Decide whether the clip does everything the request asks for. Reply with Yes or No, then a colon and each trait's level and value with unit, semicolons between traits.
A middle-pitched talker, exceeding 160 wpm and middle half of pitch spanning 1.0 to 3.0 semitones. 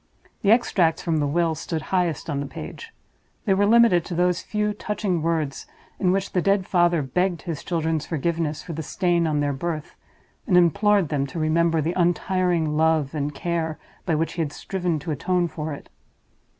Yes: medium, 170 Hz; average, 190 wpm; average, 2.7 semitones